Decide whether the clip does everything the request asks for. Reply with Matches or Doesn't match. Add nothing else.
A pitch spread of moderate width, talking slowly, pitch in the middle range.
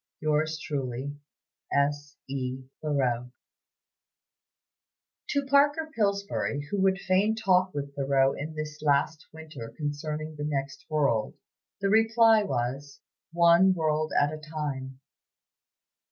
Matches